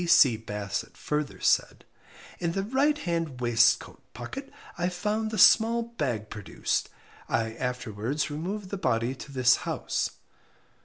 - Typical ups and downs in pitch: No, wide, 9.0 semitones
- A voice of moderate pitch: Yes, medium, 150 Hz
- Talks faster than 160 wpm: No, slow, 135 wpm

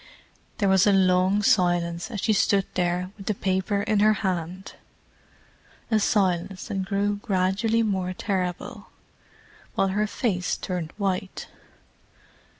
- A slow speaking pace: Yes, slow, 130 wpm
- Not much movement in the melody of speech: Yes, narrow, 2.0 semitones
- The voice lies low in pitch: No, high, 190 Hz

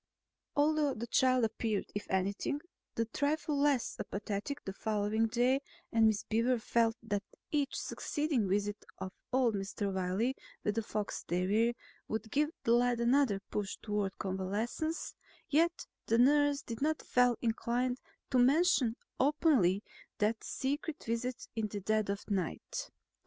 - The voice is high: Yes, high, 230 Hz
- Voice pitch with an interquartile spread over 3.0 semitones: Yes, average, 4.7 semitones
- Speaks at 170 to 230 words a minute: No, average, 140 wpm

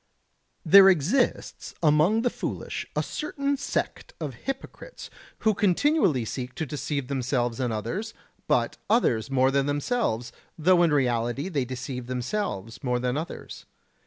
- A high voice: No, medium, 145 Hz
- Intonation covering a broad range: Yes, wide, 7.9 semitones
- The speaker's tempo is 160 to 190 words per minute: No, slow, 135 wpm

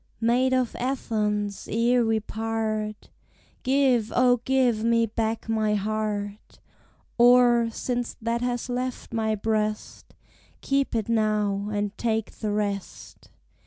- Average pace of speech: No, slow, 120 wpm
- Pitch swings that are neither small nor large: No, narrow, 2.3 semitones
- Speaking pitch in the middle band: No, high, 225 Hz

